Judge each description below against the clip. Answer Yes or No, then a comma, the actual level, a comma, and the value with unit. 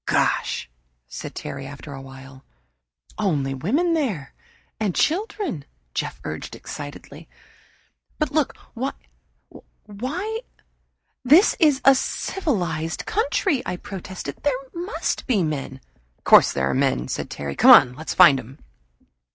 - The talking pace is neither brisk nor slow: No, slow, 125 wpm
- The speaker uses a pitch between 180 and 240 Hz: Yes, medium, 185 Hz